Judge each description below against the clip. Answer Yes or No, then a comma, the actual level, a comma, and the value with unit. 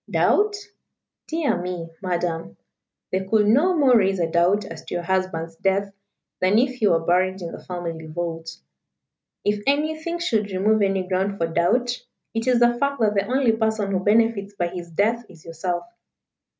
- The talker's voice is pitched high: Yes, high, 195 Hz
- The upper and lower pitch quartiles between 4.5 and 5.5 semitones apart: Yes, average, 4.8 semitones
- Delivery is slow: No, average, 175 wpm